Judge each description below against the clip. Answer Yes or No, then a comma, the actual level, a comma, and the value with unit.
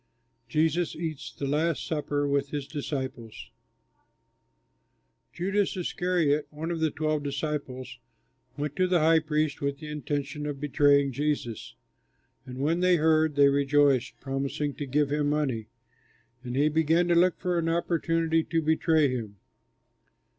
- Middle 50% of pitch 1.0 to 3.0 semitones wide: Yes, narrow, 2.5 semitones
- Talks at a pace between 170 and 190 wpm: No, average, 140 wpm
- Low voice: No, medium, 150 Hz